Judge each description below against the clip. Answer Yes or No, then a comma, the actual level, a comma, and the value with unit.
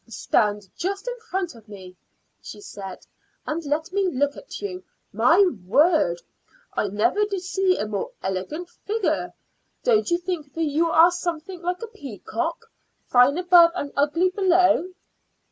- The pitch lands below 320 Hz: No, very high, 330 Hz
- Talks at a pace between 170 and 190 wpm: No, average, 150 wpm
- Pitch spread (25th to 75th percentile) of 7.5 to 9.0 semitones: Yes, wide, 8.1 semitones